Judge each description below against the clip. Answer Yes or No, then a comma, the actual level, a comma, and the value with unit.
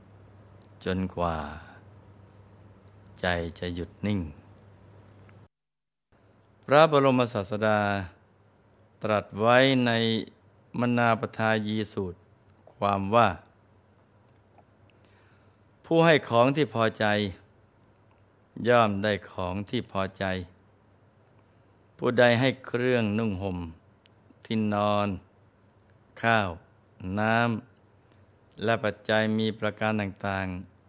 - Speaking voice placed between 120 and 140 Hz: No, low, 105 Hz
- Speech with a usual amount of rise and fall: No, narrow, 1.8 semitones